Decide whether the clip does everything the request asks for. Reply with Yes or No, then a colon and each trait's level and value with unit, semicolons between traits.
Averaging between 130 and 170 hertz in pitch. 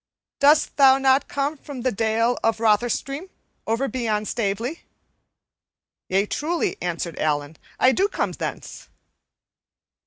No: high, 240 Hz